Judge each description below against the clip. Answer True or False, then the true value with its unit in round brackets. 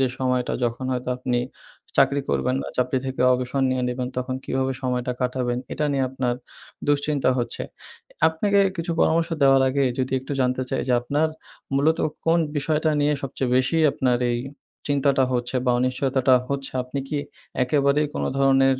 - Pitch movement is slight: True (2.0 semitones)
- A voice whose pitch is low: True (130 Hz)